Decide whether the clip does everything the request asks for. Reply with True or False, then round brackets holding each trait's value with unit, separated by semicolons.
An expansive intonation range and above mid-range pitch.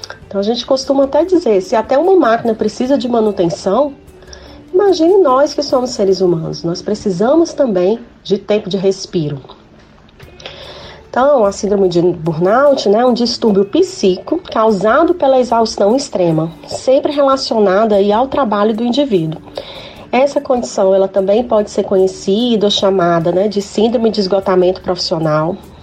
True (5.7 semitones; 215 Hz)